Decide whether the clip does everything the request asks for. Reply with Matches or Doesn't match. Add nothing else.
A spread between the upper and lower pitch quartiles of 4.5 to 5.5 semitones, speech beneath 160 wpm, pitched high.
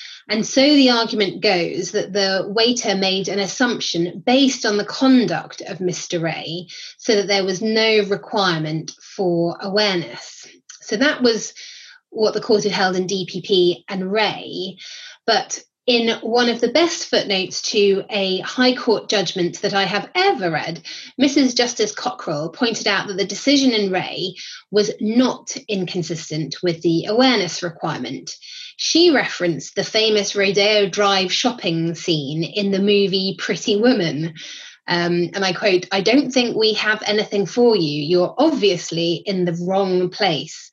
Doesn't match